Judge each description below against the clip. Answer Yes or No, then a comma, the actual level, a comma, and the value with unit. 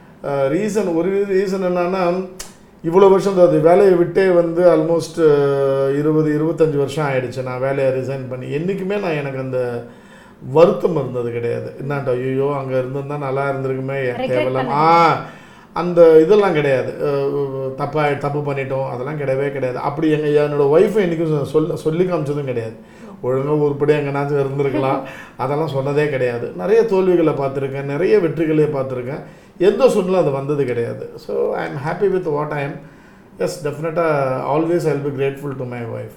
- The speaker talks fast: Yes, fast, 150 wpm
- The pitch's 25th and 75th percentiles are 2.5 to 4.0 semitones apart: Yes, average, 3.7 semitones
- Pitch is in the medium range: Yes, medium, 145 Hz